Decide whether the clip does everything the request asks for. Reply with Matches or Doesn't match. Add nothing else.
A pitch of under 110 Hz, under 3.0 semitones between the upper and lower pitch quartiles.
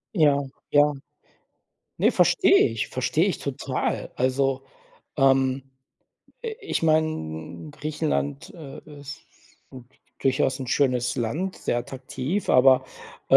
Doesn't match